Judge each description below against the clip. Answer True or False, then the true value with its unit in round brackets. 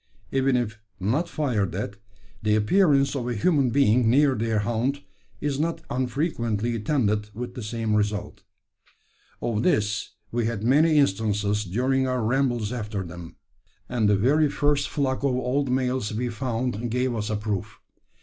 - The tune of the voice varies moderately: True (4.1 semitones)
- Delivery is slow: False (155 wpm)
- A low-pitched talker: True (120 Hz)